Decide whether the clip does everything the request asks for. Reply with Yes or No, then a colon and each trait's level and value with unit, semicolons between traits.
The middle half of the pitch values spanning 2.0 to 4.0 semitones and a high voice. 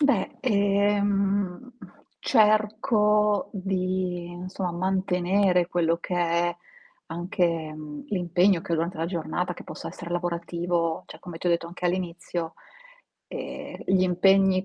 No: narrow, 2.4 semitones; medium, 180 Hz